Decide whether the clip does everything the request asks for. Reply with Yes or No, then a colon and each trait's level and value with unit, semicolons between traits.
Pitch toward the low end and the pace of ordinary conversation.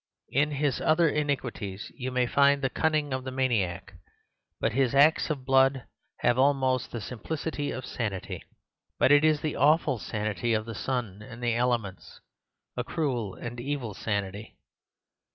Yes: low, 130 Hz; average, 150 wpm